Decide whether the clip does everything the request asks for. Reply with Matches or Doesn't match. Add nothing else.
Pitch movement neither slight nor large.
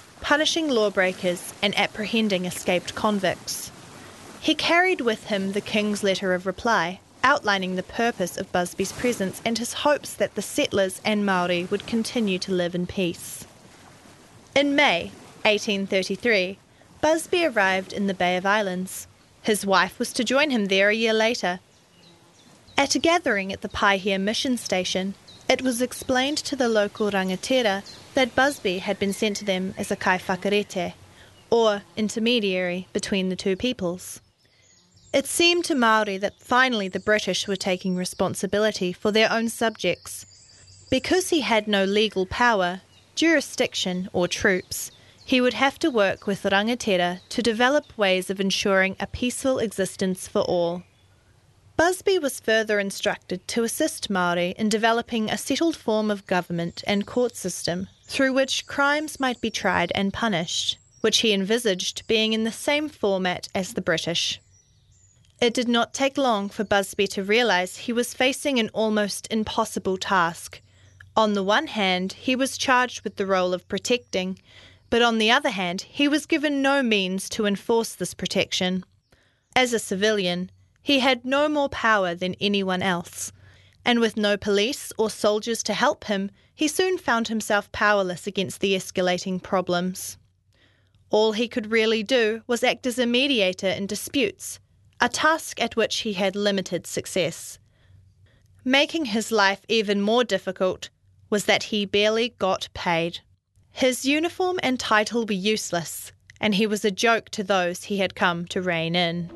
Matches